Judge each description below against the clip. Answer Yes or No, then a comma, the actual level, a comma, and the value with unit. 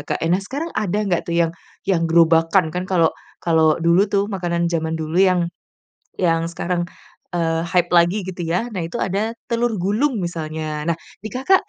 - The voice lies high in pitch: No, medium, 175 Hz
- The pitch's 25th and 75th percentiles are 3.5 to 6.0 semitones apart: No, average, 3.1 semitones